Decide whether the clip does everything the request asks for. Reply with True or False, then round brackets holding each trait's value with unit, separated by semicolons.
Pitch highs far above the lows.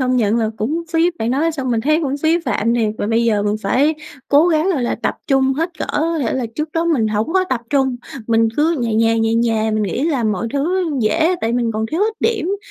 True (6.0 semitones)